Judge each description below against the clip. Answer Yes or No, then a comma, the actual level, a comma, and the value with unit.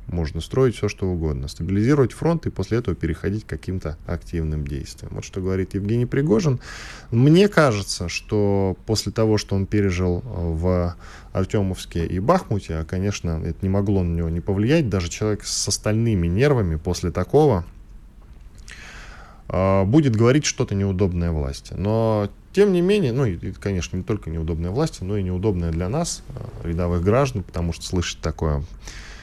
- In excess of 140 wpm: Yes, average, 155 wpm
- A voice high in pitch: No, very low, 95 Hz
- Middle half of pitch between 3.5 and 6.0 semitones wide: Yes, average, 4.3 semitones